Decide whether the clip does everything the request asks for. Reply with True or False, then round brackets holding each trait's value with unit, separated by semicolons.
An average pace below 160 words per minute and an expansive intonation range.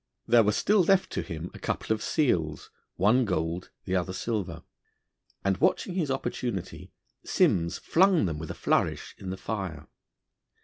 True (150 wpm; 6.5 semitones)